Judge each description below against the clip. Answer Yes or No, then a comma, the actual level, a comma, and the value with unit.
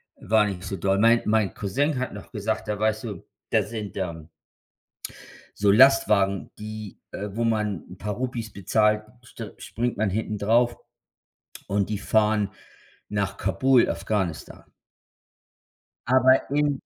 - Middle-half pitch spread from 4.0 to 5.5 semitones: No, average, 2.8 semitones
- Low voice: Yes, low, 105 Hz